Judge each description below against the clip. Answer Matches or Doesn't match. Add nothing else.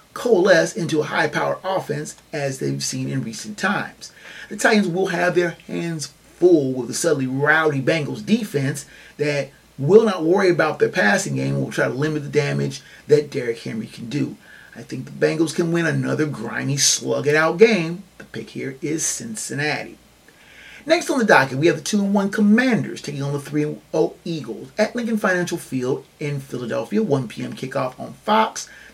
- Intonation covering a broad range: Matches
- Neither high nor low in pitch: Matches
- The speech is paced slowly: Doesn't match